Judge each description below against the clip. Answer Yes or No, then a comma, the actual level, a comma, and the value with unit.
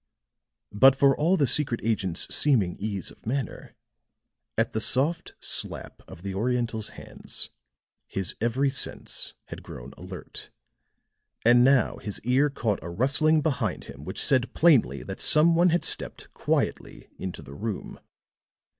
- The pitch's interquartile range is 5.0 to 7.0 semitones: Yes, wide, 5.4 semitones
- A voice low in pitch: Yes, low, 120 Hz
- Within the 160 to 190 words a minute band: No, average, 145 wpm